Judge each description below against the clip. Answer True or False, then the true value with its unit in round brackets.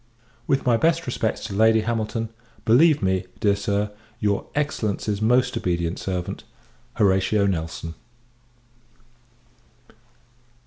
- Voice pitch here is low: True (105 Hz)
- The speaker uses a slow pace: True (100 wpm)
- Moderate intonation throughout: True (3.4 semitones)